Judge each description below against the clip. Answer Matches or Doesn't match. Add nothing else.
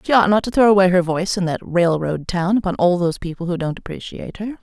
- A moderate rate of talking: Doesn't match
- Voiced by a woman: Matches